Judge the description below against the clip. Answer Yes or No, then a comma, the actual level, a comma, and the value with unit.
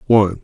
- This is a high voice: No, low, 105 Hz